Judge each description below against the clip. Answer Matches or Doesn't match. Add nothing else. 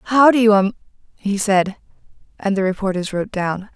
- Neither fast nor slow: Matches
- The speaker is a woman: Matches